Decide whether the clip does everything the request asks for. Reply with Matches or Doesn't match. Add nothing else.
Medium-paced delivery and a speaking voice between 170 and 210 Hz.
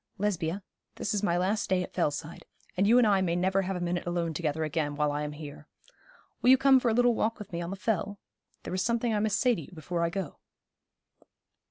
Doesn't match